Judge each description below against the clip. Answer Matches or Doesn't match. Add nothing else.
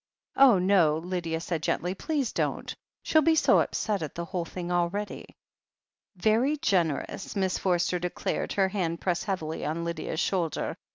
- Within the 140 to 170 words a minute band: Matches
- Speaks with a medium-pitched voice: Matches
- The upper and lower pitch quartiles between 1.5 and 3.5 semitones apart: Matches